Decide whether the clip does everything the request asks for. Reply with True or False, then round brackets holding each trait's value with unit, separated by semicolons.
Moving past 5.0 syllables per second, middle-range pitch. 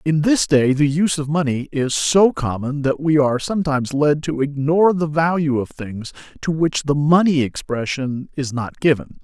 False (4.9 syllables/s; 145 Hz)